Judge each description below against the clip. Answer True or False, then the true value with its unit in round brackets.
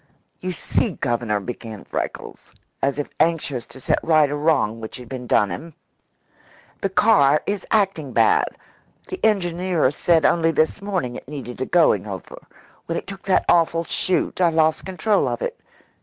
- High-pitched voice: False (160 Hz)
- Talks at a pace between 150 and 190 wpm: True (170 wpm)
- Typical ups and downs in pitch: False (6.2 semitones)